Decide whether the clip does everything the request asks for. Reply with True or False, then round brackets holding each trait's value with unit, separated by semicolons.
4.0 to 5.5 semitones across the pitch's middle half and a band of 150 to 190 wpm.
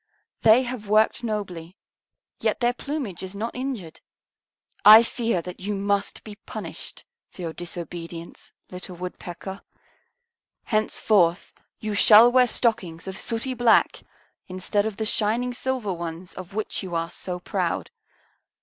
False (4.3 semitones; 135 wpm)